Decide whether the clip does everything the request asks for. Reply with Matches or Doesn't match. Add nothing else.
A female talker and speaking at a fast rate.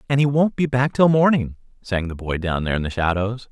Doesn't match